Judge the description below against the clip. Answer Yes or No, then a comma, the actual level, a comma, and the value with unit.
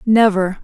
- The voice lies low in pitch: No, high, 205 Hz